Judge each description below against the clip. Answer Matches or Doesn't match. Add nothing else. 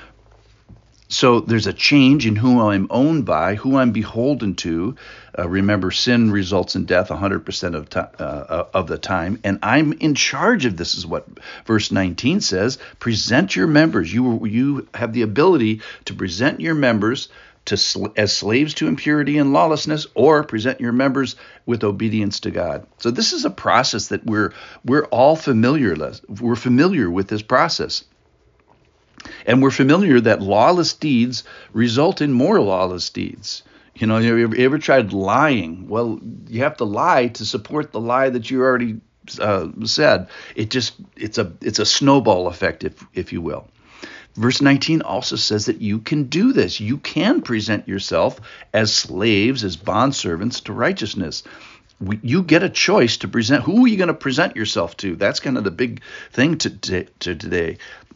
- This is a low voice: Matches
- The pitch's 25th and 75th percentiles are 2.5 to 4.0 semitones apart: Doesn't match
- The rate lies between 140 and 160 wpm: Doesn't match